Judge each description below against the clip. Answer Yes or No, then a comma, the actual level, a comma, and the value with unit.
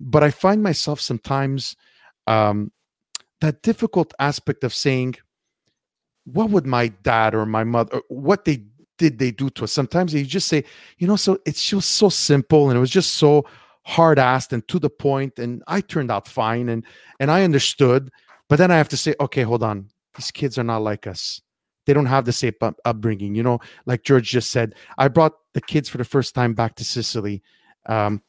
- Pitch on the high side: No, low, 135 Hz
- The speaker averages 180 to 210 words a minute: Yes, fast, 205 wpm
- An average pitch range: Yes, average, 4.8 semitones